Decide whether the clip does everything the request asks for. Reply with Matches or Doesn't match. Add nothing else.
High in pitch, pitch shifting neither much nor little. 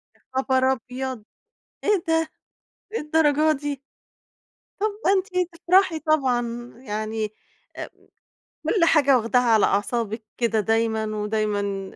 Doesn't match